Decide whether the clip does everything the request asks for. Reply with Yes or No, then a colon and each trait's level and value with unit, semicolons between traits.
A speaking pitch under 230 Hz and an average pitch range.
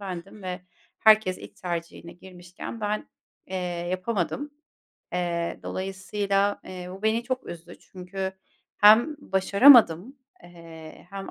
Yes: high, 190 Hz; average, 3.2 semitones